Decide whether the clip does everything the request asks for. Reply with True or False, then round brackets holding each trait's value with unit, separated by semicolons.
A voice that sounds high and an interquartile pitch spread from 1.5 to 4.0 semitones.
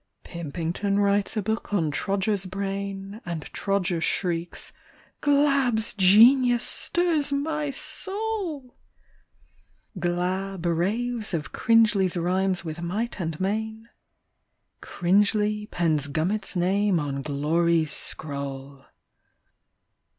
False (195 Hz; 4.6 semitones)